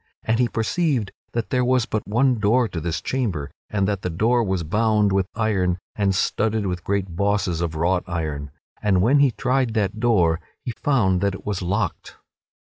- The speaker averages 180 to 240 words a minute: Yes, average, 190 wpm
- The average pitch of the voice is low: Yes, low, 100 Hz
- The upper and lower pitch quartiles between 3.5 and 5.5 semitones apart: Yes, average, 4.1 semitones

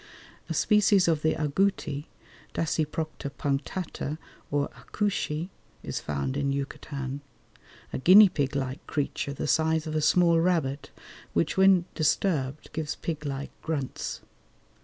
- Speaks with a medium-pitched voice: Yes, medium, 155 Hz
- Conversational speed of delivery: No, slow, 125 wpm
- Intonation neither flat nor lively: Yes, average, 3.3 semitones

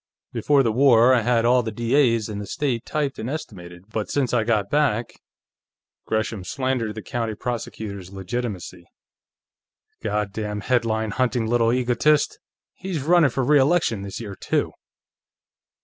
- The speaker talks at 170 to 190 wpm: No, average, 150 wpm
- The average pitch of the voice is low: Yes, low, 115 Hz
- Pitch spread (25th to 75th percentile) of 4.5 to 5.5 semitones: No, average, 3.5 semitones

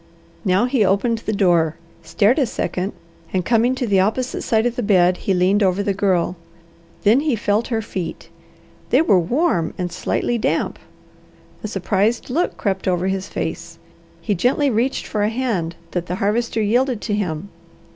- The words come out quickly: No, average, 175 wpm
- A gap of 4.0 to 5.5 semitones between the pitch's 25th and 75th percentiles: Yes, average, 4.3 semitones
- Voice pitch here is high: Yes, high, 205 Hz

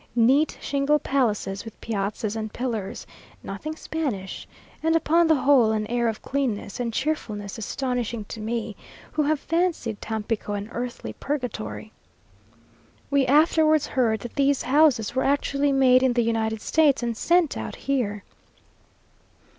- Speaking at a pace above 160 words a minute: No, average, 140 wpm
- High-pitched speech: Yes, high, 245 Hz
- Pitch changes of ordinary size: Yes, average, 4.5 semitones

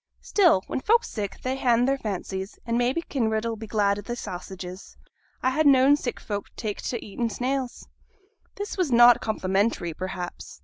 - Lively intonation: No, average, 4.5 semitones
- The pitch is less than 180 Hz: No, high, 230 Hz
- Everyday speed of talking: Yes, average, 175 wpm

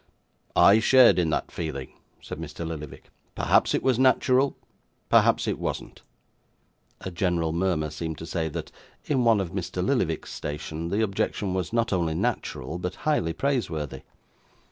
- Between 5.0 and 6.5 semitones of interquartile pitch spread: Yes, wide, 5.6 semitones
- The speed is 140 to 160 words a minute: Yes, average, 150 wpm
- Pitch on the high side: No, very low, 90 Hz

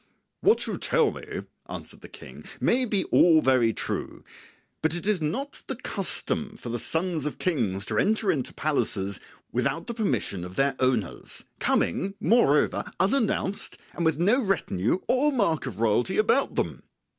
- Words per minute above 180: No, average, 160 wpm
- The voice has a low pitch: No, medium, 165 Hz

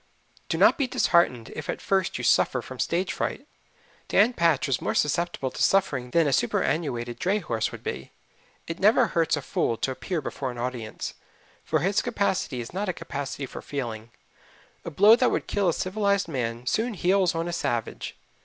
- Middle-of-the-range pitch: Yes, medium, 160 Hz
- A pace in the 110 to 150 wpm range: No, average, 190 wpm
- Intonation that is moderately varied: No, wide, 7.3 semitones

